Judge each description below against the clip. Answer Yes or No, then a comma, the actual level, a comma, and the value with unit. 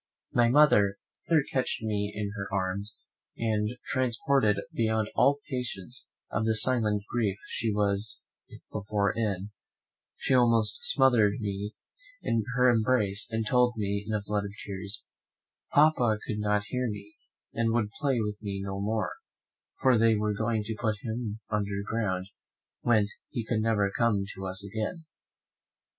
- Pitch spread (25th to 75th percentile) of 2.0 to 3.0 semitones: Yes, narrow, 2.4 semitones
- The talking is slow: No, average, 150 wpm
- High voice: No, low, 110 Hz